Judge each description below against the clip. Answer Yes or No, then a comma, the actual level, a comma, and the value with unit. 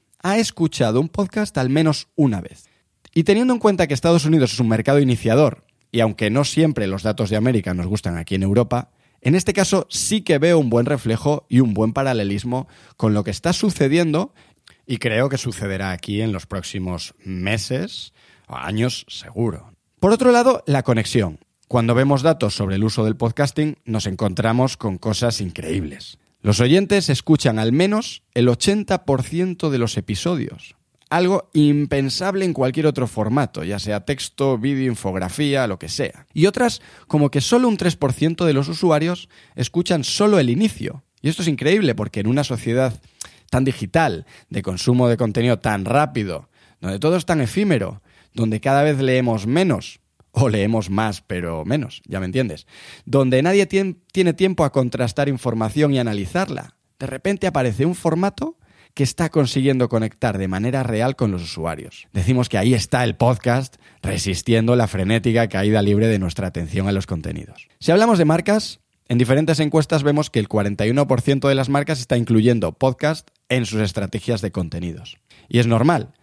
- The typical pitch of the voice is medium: No, low, 125 Hz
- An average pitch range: No, wide, 6.0 semitones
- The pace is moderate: Yes, average, 170 wpm